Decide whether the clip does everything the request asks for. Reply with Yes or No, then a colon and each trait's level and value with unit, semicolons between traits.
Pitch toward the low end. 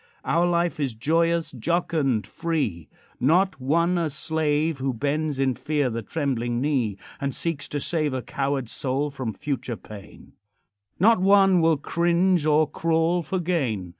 No: medium, 150 Hz